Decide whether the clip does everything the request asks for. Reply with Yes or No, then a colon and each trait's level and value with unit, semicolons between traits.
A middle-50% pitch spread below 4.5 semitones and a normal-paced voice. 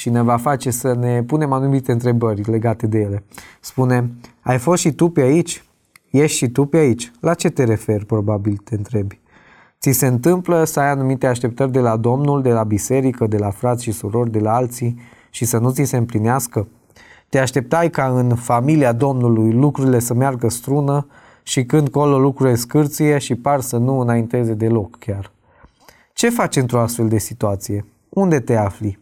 No: average, 3.5 semitones; fast, 185 wpm